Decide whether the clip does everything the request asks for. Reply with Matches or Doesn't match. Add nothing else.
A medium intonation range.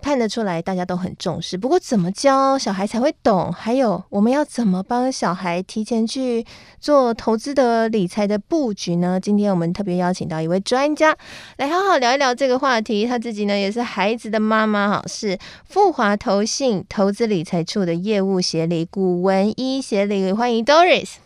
Matches